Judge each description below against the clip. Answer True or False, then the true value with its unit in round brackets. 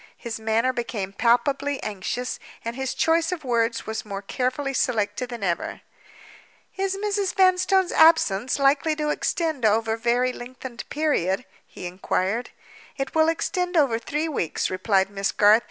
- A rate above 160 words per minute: False (150 wpm)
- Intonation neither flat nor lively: False (5.9 semitones)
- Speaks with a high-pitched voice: True (250 Hz)